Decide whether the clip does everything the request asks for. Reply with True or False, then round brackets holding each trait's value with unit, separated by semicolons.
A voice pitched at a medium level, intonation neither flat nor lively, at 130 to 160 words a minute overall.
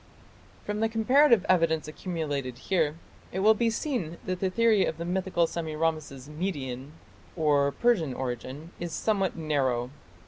True (165 Hz; 4.9 semitones; 140 wpm)